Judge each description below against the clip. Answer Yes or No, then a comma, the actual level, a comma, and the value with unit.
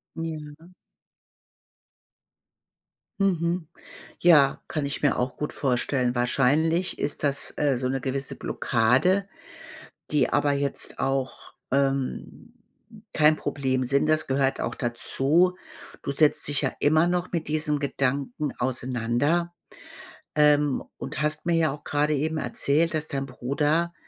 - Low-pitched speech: No, medium, 145 Hz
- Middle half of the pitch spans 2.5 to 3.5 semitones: Yes, average, 2.8 semitones